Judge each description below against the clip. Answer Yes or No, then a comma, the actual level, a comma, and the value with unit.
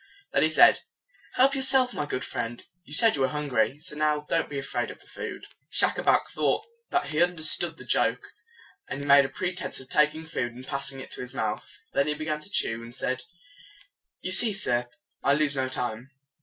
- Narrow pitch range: No, average, 4.1 semitones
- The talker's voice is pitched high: No, medium, 145 Hz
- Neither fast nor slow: No, fast, 210 wpm